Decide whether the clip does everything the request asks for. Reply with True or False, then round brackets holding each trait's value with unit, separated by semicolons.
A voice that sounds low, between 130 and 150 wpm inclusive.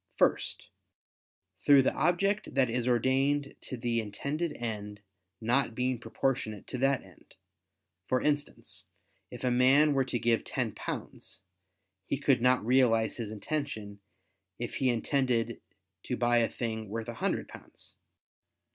True (125 Hz; 140 wpm)